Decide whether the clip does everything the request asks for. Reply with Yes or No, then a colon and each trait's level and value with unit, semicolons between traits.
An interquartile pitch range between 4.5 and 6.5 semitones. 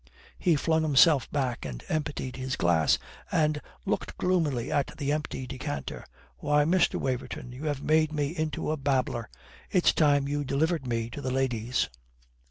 No: average, 3.3 semitones